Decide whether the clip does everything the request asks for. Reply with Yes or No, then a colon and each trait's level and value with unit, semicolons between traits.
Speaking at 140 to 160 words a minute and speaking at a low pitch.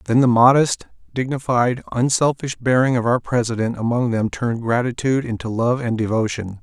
Yes: average, 155 wpm; low, 120 Hz